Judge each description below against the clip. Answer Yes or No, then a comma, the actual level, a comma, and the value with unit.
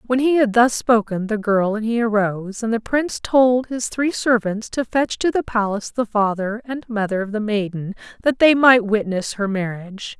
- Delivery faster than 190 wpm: Yes, fast, 205 wpm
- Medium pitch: No, high, 225 Hz